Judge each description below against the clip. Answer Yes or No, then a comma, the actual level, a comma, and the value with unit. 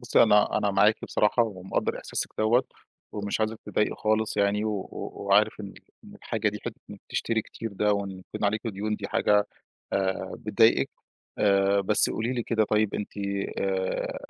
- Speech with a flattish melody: Yes, narrow, 1.5 semitones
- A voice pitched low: Yes, low, 105 Hz